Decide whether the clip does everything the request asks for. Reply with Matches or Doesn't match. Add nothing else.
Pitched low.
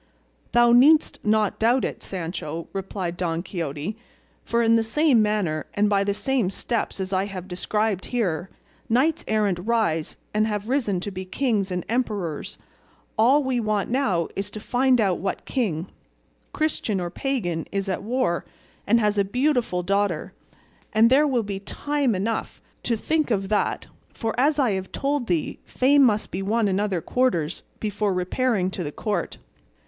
Doesn't match